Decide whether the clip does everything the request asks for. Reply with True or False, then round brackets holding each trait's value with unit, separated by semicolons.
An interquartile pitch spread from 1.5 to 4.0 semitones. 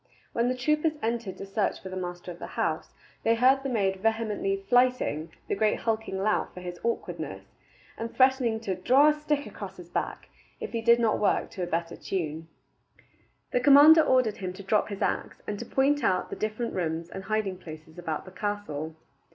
False (4.9 semitones)